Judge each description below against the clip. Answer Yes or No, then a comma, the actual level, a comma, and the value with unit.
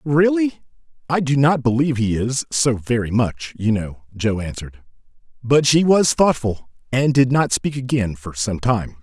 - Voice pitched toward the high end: No, low, 125 Hz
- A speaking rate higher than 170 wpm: No, average, 165 wpm